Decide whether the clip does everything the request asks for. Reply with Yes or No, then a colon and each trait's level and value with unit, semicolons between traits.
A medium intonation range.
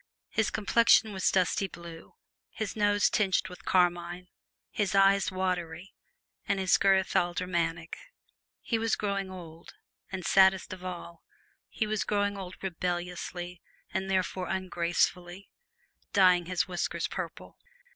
No: narrow, 1.9 semitones